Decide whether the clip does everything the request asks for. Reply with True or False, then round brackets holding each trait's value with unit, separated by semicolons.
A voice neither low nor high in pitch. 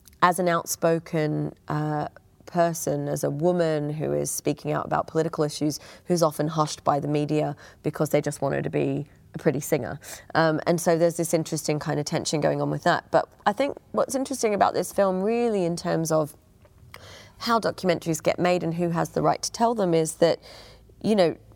True (155 Hz)